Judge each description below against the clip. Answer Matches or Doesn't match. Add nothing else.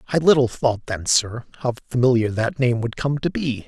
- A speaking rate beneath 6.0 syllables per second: Matches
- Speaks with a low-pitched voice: Matches